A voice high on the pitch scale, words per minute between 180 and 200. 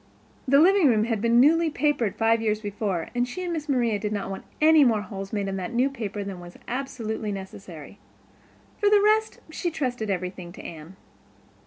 Yes: high, 225 Hz; average, 195 wpm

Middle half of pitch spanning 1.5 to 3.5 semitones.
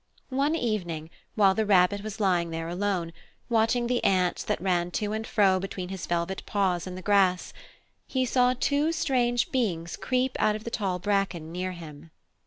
No: average, 4.4 semitones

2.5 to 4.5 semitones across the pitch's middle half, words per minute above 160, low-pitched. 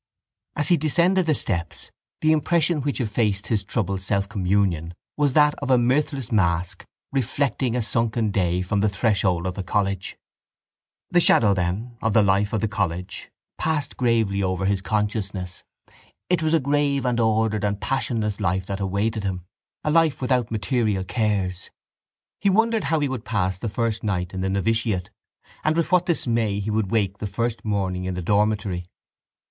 No: average, 4.9 semitones; average, 170 wpm; low, 105 Hz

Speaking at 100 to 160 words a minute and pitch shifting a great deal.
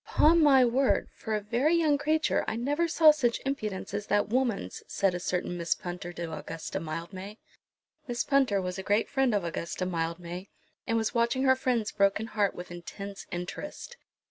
No: average, 180 wpm; wide, 6.6 semitones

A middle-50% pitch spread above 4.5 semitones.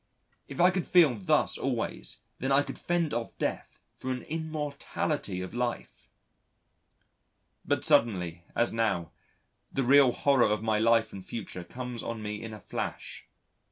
Yes: average, 4.9 semitones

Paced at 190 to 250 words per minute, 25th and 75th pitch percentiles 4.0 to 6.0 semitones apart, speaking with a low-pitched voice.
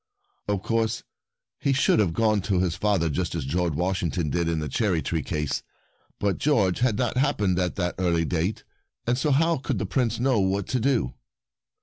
Yes: average, 195 wpm; average, 5.0 semitones; very low, 95 Hz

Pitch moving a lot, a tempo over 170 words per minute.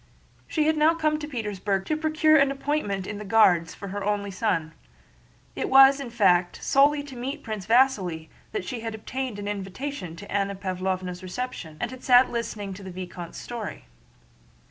Yes: wide, 6.2 semitones; average, 180 wpm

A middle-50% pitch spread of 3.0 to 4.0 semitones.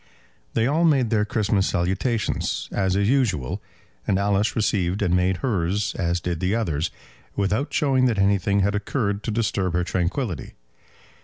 Yes: average, 3.5 semitones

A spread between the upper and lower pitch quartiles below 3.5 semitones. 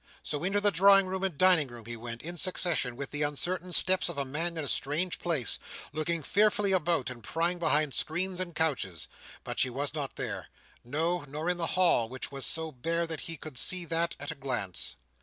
No: average, 4.6 semitones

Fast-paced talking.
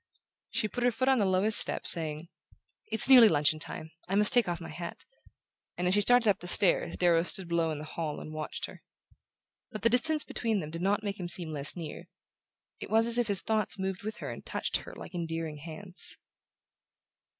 Yes: fast, 215 wpm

